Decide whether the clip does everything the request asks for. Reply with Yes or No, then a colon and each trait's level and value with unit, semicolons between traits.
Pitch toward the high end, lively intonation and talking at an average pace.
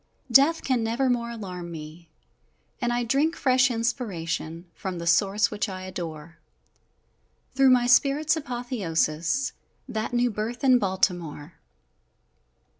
No: high, 225 Hz; wide, 6.5 semitones; slow, 120 wpm